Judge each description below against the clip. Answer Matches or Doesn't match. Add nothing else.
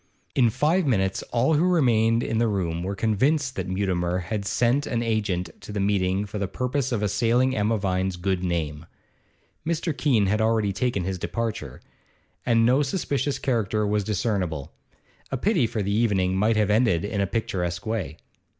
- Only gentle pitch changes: Doesn't match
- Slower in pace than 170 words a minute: Doesn't match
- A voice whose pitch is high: Doesn't match